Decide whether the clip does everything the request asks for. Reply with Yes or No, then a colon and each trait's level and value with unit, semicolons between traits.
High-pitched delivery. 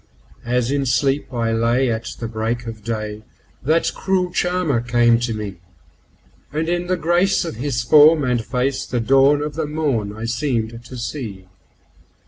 No: low, 125 Hz